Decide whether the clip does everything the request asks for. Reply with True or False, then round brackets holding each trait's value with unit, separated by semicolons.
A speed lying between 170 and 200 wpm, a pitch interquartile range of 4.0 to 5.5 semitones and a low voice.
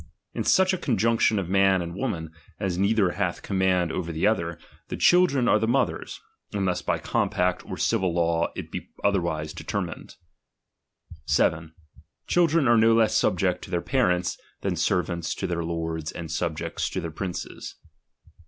False (160 wpm; 4.8 semitones; 90 Hz)